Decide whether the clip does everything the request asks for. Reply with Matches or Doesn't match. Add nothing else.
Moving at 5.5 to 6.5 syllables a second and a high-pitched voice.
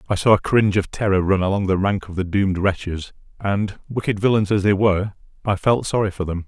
Doesn't match